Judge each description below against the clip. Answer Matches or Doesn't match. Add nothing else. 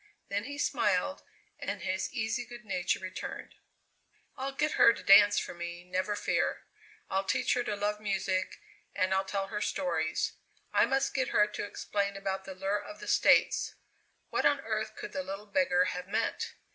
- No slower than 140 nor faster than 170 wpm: Doesn't match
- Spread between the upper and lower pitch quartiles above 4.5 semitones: Doesn't match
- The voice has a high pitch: Matches